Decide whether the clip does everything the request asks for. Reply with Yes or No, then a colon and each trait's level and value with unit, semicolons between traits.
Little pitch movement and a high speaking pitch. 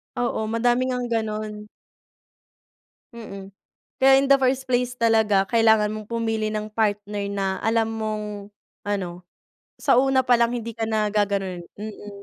Yes: narrow, 2.2 semitones; high, 220 Hz